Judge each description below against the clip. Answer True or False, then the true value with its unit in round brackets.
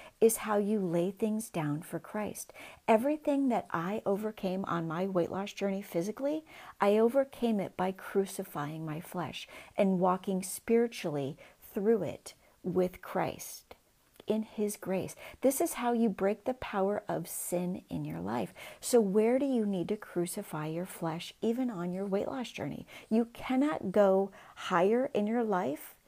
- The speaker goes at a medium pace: True (160 wpm)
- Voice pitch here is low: False (200 Hz)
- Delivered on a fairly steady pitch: False (4.0 semitones)